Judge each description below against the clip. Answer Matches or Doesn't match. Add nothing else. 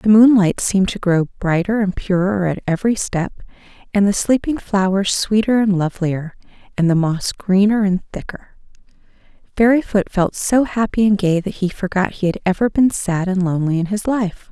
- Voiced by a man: Doesn't match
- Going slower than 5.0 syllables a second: Doesn't match